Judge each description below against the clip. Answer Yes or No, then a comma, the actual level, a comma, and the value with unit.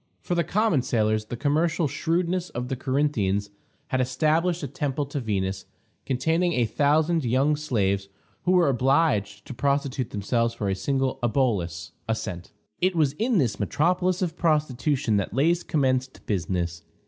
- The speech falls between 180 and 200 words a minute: No, average, 155 wpm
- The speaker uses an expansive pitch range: Yes, wide, 6.5 semitones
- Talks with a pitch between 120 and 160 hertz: Yes, low, 135 Hz